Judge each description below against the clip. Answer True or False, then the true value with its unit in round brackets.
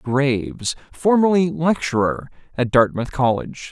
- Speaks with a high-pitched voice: False (140 Hz)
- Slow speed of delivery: True (95 wpm)